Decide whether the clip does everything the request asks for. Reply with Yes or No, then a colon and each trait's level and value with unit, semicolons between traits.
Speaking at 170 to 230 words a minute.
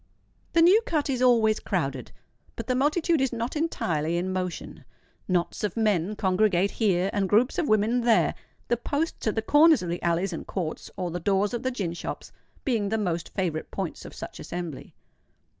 Yes: average, 185 wpm